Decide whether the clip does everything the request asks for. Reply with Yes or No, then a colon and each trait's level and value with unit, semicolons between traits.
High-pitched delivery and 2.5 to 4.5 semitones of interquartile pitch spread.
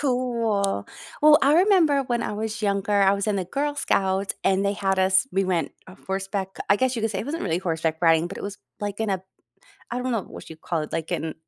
Yes: high, 200 Hz; average, 4.2 semitones